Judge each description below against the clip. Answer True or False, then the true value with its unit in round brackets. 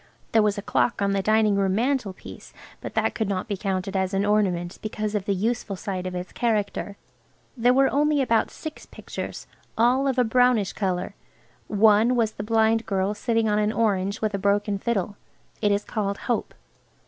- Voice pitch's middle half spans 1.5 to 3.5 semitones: True (2.5 semitones)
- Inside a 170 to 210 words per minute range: True (185 wpm)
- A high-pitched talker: True (210 Hz)